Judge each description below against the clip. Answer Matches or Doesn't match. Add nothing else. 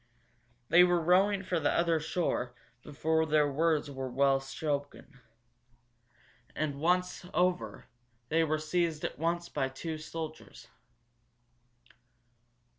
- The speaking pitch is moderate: Matches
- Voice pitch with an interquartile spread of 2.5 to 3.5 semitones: Matches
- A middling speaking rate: Doesn't match